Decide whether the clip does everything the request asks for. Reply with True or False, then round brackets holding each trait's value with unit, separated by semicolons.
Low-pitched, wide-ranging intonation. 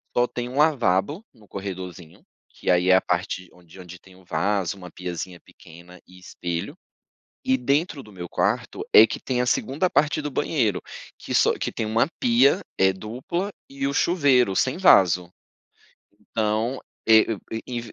True (110 Hz; 6.8 semitones)